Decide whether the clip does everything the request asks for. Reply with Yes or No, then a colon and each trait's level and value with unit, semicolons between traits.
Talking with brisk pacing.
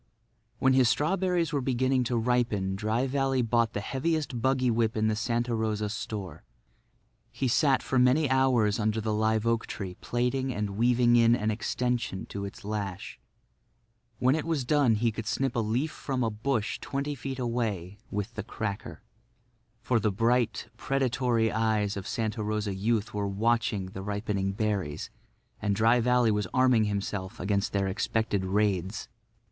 No: average, 165 wpm